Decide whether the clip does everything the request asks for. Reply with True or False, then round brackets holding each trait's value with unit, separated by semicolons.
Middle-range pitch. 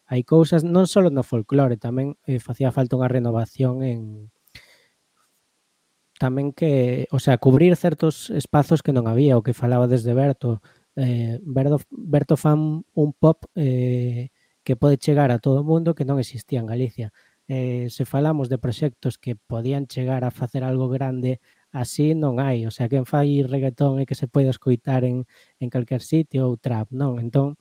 False (130 Hz)